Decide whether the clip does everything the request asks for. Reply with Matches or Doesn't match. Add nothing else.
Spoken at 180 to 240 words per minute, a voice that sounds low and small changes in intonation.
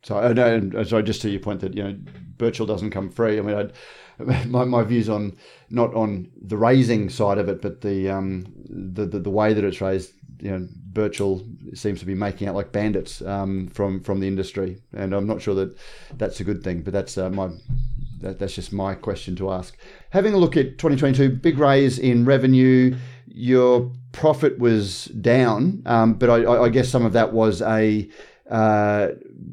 Doesn't match